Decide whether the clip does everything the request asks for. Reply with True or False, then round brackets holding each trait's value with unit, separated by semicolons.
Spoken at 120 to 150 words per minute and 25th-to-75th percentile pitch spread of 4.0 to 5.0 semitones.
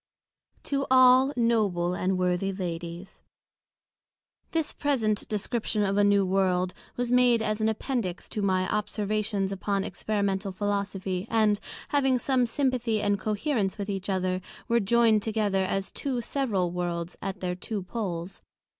False (140 wpm; 3.6 semitones)